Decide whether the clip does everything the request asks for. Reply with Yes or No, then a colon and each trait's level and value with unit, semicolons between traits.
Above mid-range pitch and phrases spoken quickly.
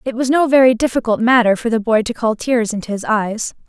Yes: high, 235 Hz; fast, 245 wpm